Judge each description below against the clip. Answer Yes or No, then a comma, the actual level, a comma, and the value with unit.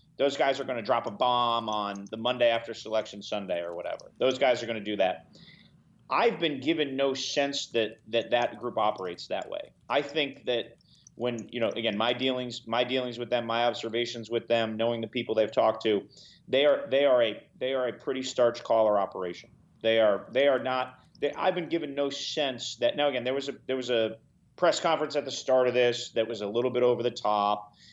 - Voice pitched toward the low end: Yes, low, 120 Hz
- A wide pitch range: No, narrow, 2.5 semitones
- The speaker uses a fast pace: Yes, fast, 225 wpm